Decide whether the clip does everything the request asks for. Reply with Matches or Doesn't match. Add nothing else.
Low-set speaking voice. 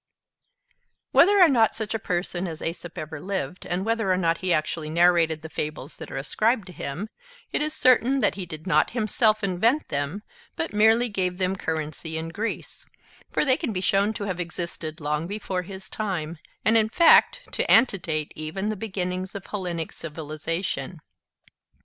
Doesn't match